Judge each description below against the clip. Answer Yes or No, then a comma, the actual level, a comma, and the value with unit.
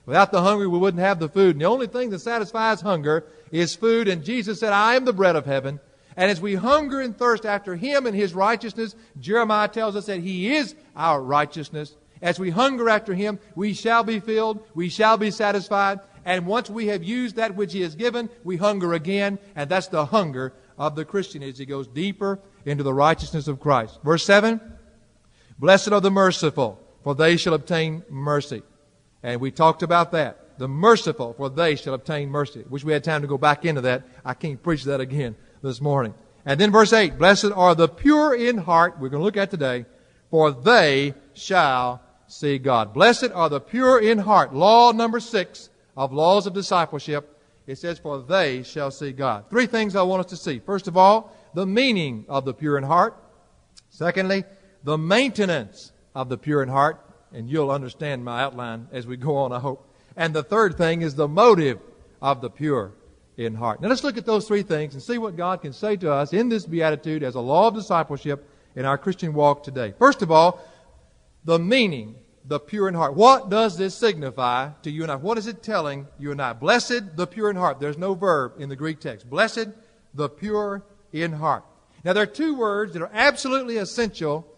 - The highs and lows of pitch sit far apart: Yes, wide, 6.5 semitones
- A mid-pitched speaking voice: Yes, medium, 170 Hz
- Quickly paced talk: Yes, fast, 210 wpm